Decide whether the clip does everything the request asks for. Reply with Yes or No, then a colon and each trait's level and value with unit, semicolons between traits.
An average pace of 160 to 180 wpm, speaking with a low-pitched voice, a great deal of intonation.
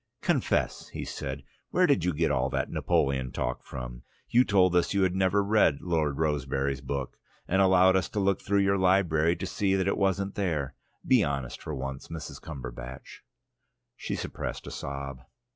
Yes: average, 175 wpm; very low, 80 Hz; wide, 6.0 semitones